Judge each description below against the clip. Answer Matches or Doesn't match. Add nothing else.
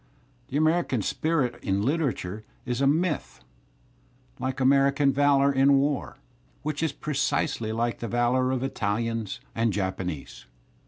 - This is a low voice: Matches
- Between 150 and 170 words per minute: Doesn't match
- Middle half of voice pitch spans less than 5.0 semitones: Matches